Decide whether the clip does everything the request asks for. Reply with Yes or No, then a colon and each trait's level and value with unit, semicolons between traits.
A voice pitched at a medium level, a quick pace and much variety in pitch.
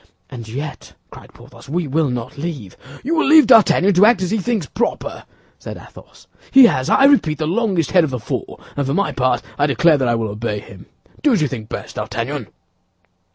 Yes: medium, 150 Hz; fast, 210 wpm; wide, 8.1 semitones